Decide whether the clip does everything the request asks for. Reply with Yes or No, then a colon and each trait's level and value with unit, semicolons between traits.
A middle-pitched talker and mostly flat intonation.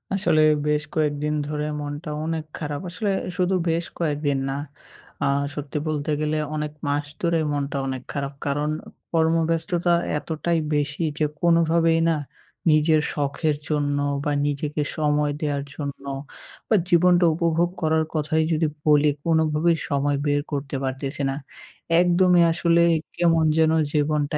Yes: medium, 155 Hz; narrow, 2.2 semitones